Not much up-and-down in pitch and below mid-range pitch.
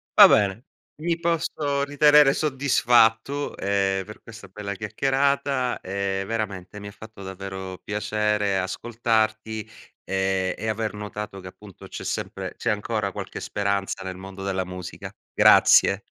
No: average, 3.5 semitones; low, 105 Hz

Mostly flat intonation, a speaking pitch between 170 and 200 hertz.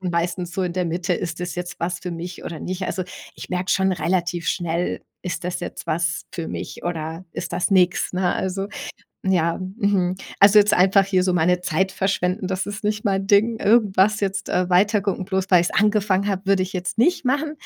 Yes: narrow, 2.0 semitones; medium, 185 Hz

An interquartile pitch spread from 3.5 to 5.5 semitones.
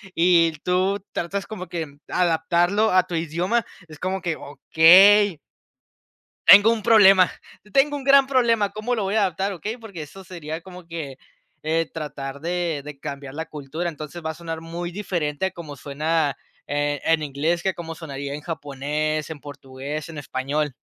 Yes: average, 4.2 semitones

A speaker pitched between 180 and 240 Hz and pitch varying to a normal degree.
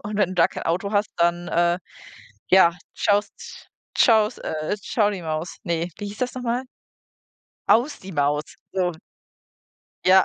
Yes: high, 190 Hz; average, 3.5 semitones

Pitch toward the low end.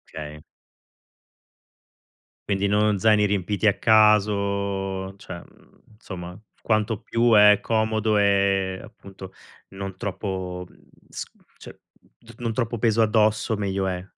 Yes: low, 100 Hz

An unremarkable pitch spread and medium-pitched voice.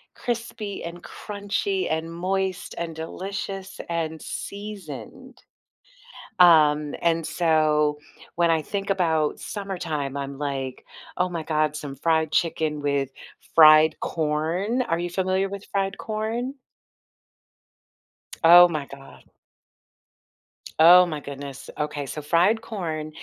Yes: average, 4.1 semitones; medium, 165 Hz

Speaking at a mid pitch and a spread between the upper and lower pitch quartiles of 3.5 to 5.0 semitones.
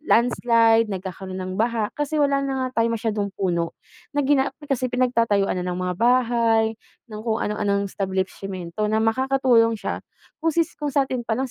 No: high, 230 Hz; average, 4.2 semitones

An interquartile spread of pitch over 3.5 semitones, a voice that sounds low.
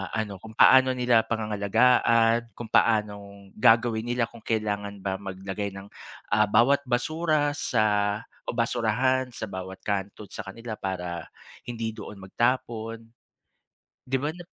No: average, 3.0 semitones; low, 110 Hz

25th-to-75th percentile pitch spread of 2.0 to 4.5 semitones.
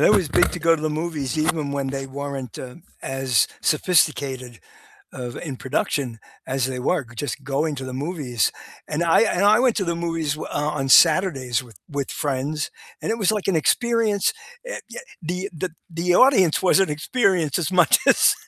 No: average, 5.0 semitones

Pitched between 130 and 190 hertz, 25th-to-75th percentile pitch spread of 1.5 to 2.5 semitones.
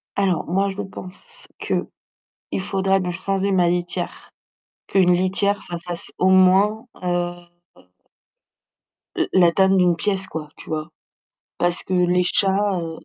Yes: medium, 185 Hz; narrow, 1.8 semitones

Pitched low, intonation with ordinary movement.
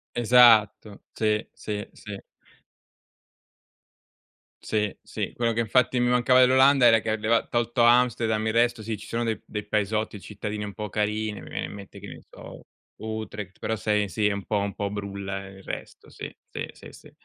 No: low, 110 Hz; narrow, 2.2 semitones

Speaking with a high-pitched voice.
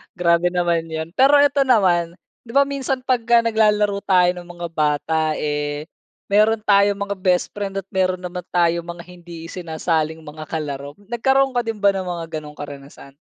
No: medium, 180 Hz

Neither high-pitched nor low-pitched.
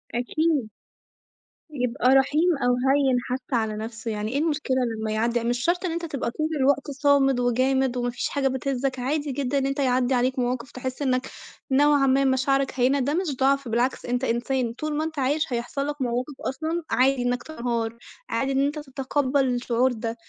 No: very high, 265 Hz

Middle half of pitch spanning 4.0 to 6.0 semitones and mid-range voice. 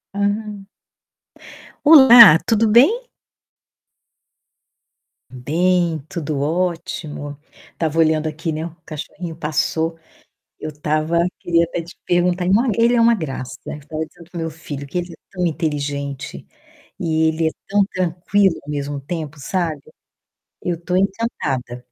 No: average, 3.3 semitones; medium, 165 Hz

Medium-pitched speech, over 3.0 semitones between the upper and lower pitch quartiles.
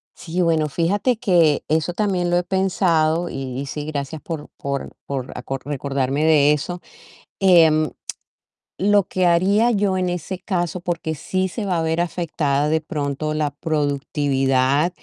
Yes: medium, 160 Hz; average, 3.7 semitones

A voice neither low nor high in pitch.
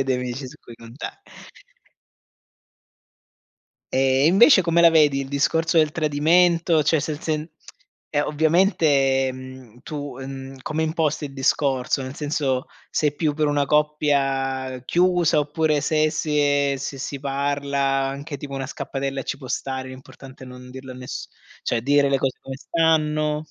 Yes: medium, 145 Hz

